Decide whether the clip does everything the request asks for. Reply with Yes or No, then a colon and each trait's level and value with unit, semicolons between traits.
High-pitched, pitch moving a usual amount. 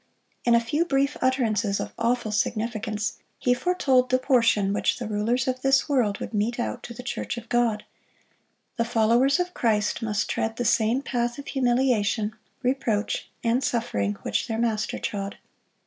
Yes: high, 235 Hz; average, 3.0 semitones